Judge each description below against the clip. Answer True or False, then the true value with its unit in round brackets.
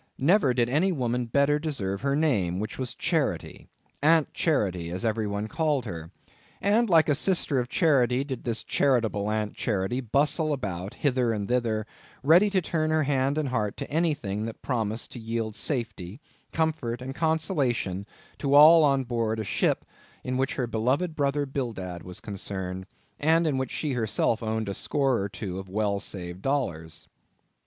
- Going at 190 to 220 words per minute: False (165 wpm)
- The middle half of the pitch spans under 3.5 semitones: False (5.6 semitones)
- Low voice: True (125 Hz)